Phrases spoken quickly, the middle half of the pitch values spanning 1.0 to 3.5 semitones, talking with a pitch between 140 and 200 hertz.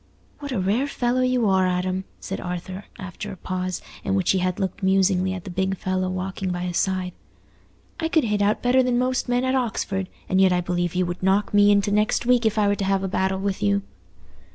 Yes: fast, 230 wpm; narrow, 2.5 semitones; high, 190 Hz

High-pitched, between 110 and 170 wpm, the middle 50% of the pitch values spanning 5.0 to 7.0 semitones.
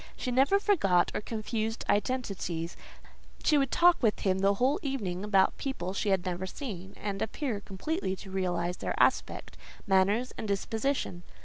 Yes: high, 205 Hz; average, 155 wpm; wide, 5.4 semitones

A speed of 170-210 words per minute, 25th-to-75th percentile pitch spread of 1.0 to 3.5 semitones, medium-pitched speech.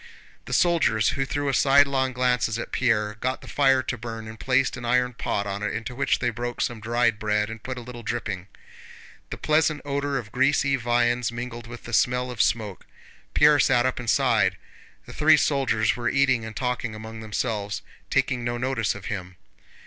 No: average, 190 wpm; average, 2.9 semitones; low, 120 Hz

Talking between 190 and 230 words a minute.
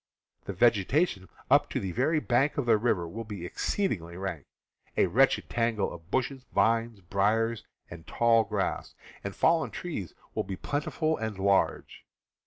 No: average, 155 wpm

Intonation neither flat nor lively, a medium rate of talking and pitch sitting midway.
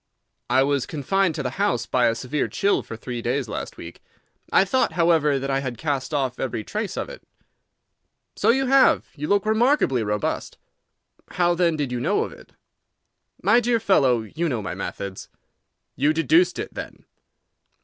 No: wide, 7.7 semitones; average, 175 wpm; medium, 145 Hz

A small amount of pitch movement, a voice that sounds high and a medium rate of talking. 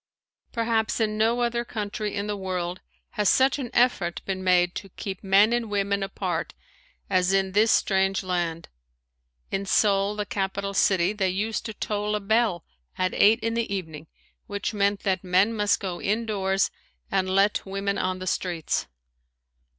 Yes: narrow, 2.2 semitones; high, 200 Hz; average, 165 wpm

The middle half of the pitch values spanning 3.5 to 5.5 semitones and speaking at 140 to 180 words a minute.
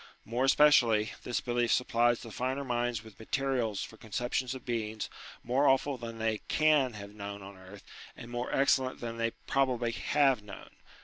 No: average, 2.9 semitones; average, 175 wpm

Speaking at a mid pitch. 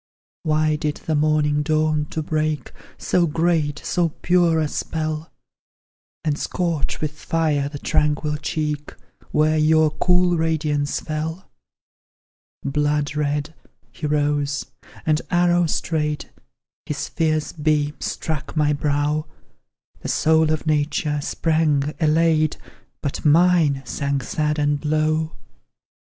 Yes: medium, 155 Hz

